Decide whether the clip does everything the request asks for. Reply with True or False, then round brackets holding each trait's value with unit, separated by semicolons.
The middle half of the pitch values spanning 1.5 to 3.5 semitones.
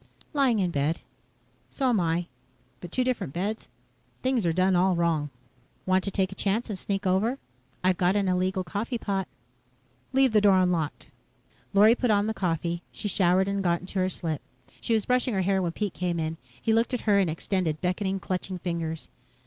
True (3.0 semitones)